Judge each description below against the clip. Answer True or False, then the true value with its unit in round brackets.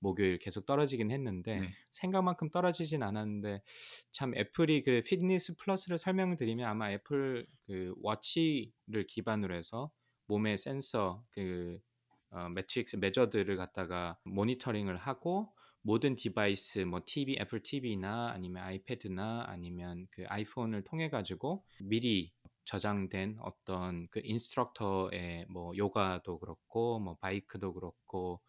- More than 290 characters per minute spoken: True (305 characters per minute)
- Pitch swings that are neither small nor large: True (4.9 semitones)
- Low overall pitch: True (105 Hz)